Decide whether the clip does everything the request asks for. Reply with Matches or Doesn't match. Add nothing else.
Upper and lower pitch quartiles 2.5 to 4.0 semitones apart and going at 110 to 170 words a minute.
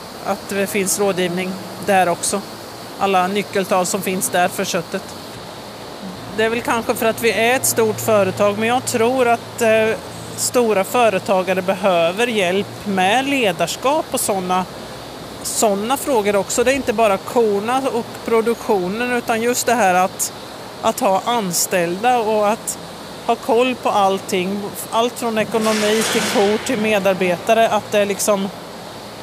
Matches